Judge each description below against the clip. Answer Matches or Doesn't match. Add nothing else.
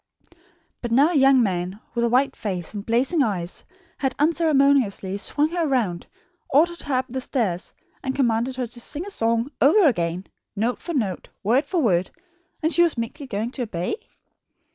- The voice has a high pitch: Matches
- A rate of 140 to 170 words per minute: Doesn't match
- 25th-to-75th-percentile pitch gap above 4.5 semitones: Matches